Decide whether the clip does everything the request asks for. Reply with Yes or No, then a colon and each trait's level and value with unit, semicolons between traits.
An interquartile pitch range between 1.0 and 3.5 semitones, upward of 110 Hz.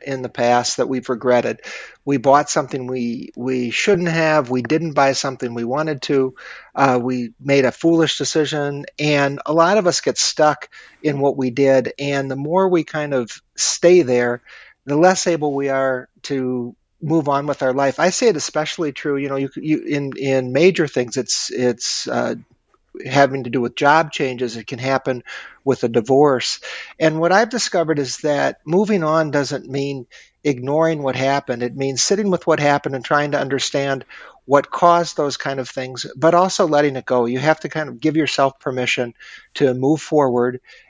Yes: average, 3.2 semitones; medium, 140 Hz